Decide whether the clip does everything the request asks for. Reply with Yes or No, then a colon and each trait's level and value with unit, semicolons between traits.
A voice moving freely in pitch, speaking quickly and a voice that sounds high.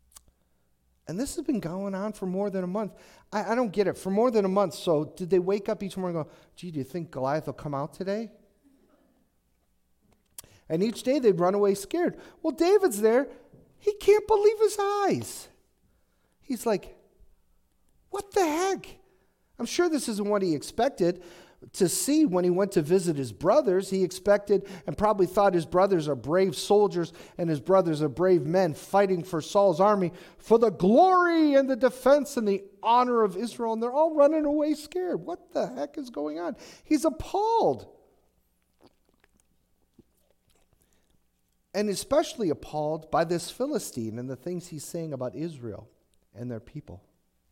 No: wide, 7.1 semitones; average, 170 wpm; high, 195 Hz